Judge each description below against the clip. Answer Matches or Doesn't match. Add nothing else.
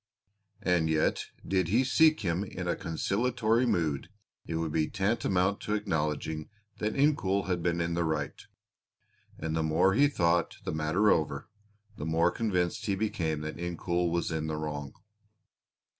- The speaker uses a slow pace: Doesn't match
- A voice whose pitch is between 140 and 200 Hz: Doesn't match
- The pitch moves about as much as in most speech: Matches